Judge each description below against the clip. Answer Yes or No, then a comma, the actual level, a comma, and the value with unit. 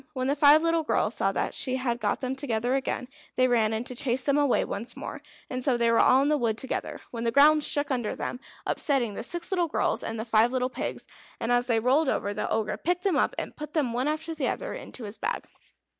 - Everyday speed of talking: No, fast, 250 wpm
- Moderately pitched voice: No, very high, 255 Hz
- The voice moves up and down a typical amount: Yes, average, 4.0 semitones